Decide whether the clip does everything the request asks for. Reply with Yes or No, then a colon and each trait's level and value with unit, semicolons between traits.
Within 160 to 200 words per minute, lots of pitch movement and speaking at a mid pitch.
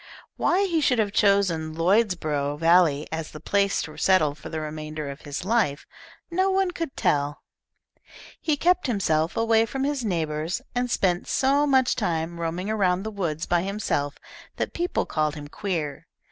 Yes: average, 165 wpm; wide, 6.7 semitones; medium, 180 Hz